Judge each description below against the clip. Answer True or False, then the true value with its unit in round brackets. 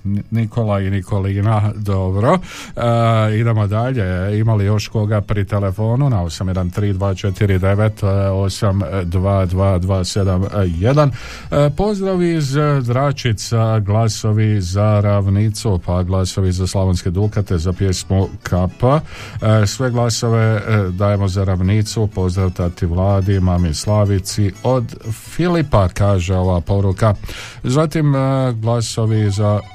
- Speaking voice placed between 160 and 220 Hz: False (105 Hz)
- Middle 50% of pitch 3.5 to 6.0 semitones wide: False (2.8 semitones)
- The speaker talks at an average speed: False (100 wpm)